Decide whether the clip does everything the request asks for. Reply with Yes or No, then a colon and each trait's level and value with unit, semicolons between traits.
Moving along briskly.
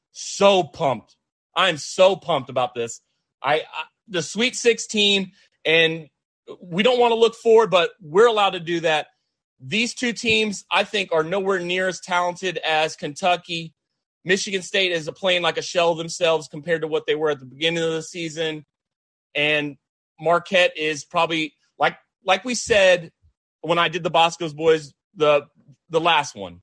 No: average, 175 wpm